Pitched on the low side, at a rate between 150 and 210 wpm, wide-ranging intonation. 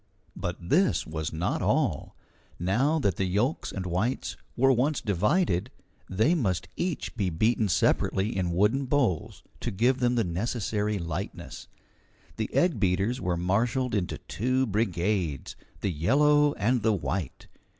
No: low, 105 Hz; average, 140 wpm; wide, 5.9 semitones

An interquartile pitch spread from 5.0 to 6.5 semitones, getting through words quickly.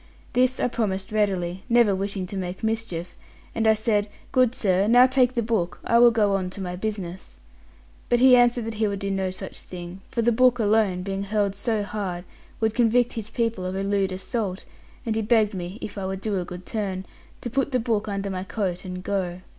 No: average, 3.3 semitones; fast, 220 wpm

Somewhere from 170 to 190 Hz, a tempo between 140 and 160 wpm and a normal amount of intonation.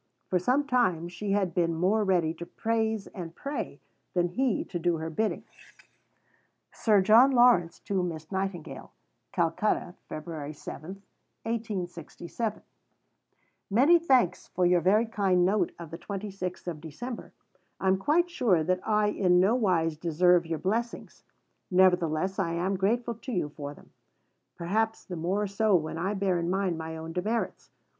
Yes: medium, 185 Hz; average, 150 wpm; average, 4.1 semitones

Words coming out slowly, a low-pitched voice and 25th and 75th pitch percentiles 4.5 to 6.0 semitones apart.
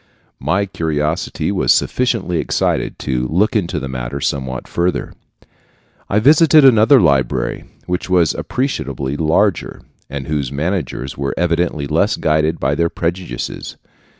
Yes: slow, 125 wpm; very low, 80 Hz; wide, 5.4 semitones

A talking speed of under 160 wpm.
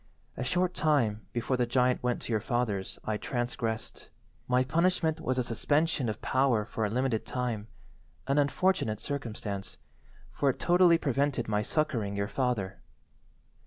Yes: average, 140 wpm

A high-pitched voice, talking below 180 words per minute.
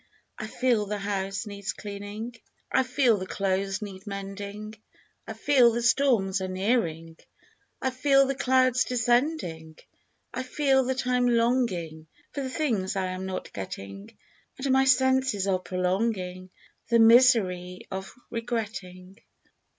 Yes: high, 210 Hz; slow, 135 wpm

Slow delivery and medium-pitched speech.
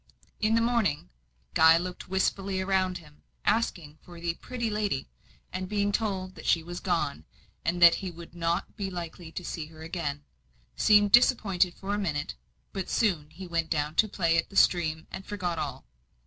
No: average, 180 wpm; medium, 180 Hz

